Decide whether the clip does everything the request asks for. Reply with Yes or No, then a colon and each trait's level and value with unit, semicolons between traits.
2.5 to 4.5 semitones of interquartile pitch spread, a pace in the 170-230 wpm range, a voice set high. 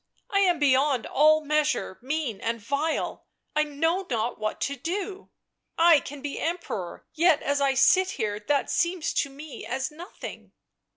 No: average, 3.7 semitones; average, 160 wpm; very high, 295 Hz